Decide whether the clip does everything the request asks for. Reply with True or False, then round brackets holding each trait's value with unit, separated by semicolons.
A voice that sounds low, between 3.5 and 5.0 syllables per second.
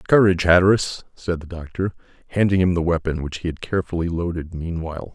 False (85 Hz; 6.3 syllables/s)